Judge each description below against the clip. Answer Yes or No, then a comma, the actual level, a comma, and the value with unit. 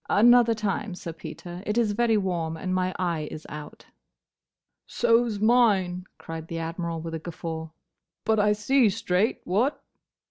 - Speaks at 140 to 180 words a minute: Yes, average, 155 wpm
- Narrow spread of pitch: No, average, 4.9 semitones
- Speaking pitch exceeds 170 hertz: Yes, medium, 185 Hz